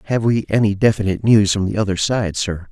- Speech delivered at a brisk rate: Yes, fast, 220 wpm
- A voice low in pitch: Yes, low, 100 Hz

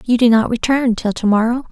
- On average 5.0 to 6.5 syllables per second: Yes, 5.7 syllables/s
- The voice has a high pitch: Yes, high, 235 Hz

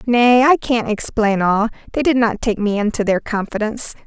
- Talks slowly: No, average, 190 wpm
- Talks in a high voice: Yes, high, 225 Hz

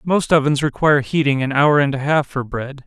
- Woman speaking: No, male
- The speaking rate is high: Yes, fast, 230 wpm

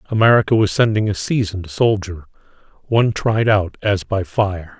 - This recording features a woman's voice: No, male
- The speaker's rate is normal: Yes, average, 150 wpm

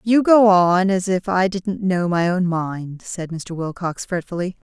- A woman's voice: Yes, female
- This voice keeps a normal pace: Yes, average, 190 wpm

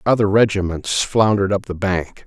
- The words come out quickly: No, average, 160 wpm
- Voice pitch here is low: Yes, low, 100 Hz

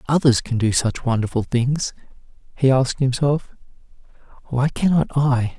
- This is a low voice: Yes, low, 130 Hz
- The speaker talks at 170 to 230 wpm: No, average, 140 wpm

